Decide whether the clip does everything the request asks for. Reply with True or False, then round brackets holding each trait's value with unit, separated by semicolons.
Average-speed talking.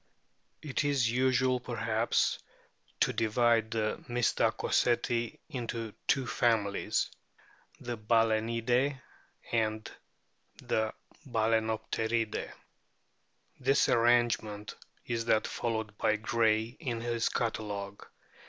False (85 wpm)